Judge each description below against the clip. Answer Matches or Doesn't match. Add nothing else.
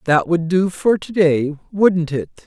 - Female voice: Doesn't match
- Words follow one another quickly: Doesn't match